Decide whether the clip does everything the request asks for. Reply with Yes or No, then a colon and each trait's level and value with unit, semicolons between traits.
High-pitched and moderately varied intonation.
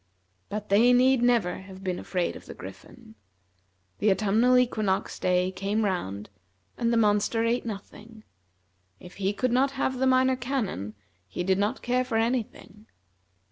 Yes: high, 215 Hz; average, 4.5 semitones